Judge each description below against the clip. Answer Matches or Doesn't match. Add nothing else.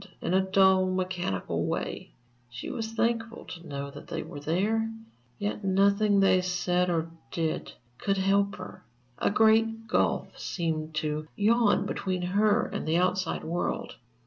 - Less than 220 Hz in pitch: Matches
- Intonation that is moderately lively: Matches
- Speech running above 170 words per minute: Doesn't match